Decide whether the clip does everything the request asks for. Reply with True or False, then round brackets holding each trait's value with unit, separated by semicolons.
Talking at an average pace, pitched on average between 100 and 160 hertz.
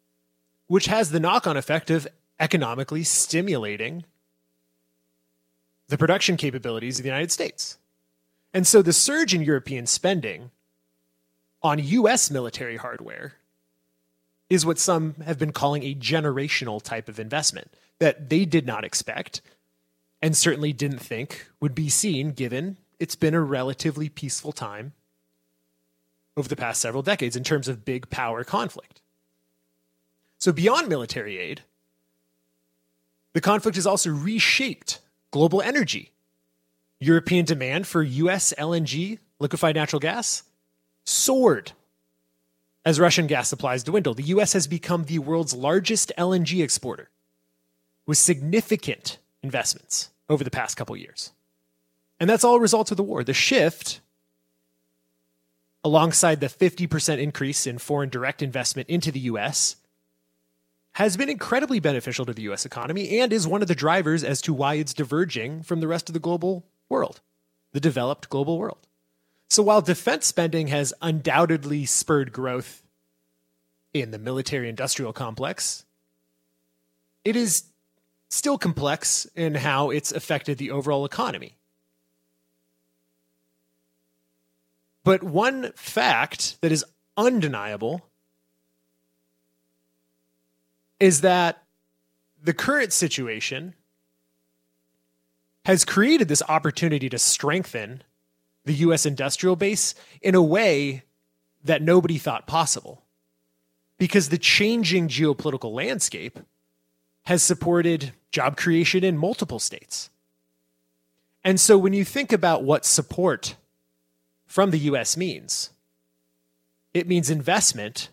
False (120 wpm; 135 Hz)